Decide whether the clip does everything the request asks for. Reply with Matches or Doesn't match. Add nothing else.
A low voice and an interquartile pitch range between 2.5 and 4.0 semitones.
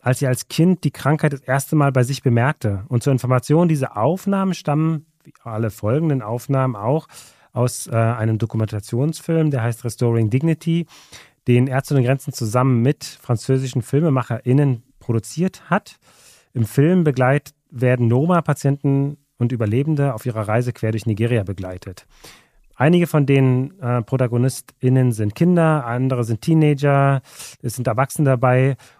Matches